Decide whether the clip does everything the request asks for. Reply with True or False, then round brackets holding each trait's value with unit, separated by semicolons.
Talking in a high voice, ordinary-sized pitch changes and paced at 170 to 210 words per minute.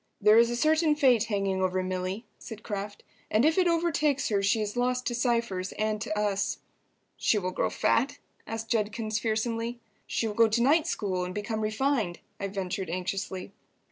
True (220 Hz; 3.5 semitones; 180 wpm)